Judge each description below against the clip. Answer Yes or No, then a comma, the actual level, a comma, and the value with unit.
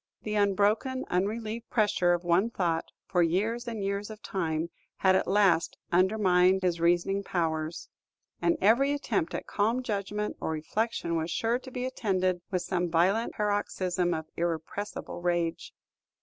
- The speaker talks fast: No, average, 150 wpm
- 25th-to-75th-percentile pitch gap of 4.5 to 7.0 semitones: No, average, 3.7 semitones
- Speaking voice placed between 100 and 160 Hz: No, high, 190 Hz